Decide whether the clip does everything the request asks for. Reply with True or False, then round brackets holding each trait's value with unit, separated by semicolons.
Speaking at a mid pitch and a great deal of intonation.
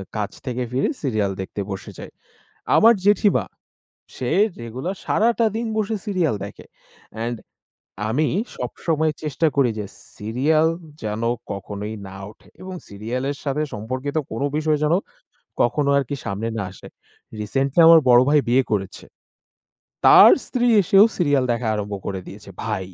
False (130 Hz; 6.7 semitones)